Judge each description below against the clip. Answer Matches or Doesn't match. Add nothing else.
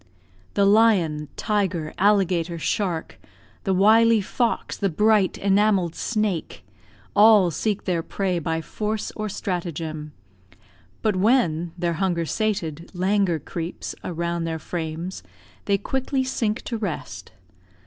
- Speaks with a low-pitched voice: Doesn't match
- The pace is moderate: Doesn't match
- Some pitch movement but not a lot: Matches